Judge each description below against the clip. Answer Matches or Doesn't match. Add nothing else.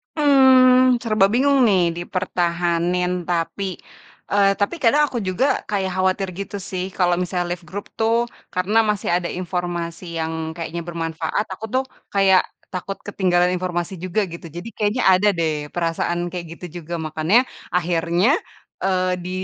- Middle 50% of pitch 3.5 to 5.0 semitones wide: Doesn't match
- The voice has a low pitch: Doesn't match